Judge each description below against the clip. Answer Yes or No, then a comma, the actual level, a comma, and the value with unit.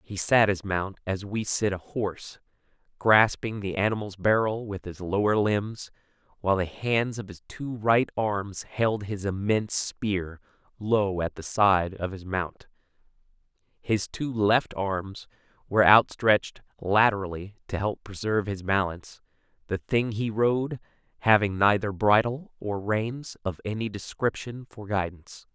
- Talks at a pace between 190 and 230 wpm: No, average, 145 wpm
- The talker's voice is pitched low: Yes, low, 105 Hz